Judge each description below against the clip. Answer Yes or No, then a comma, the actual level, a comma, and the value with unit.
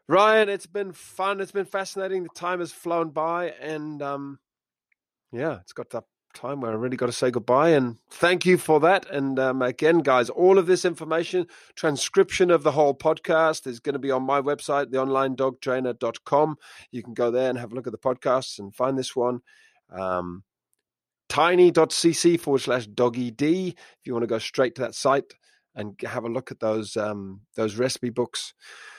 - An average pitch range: No, wide, 5.7 semitones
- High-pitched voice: No, medium, 140 Hz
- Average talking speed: Yes, average, 185 wpm